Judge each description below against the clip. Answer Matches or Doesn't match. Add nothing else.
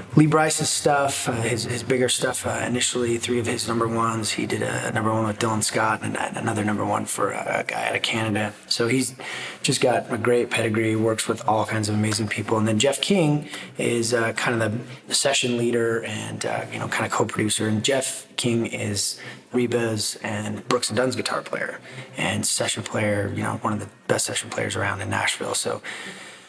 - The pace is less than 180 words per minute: Doesn't match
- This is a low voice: Matches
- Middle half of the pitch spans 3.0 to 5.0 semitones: Doesn't match